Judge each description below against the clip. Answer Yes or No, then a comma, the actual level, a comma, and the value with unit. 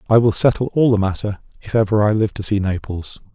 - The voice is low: Yes, low, 105 Hz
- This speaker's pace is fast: Yes, fast, 235 wpm